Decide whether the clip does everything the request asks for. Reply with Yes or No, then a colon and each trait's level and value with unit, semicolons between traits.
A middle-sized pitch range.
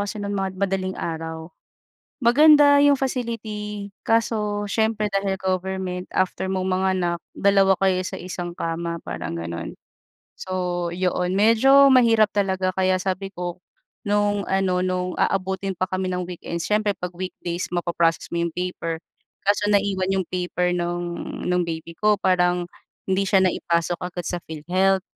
No: narrow, 2.3 semitones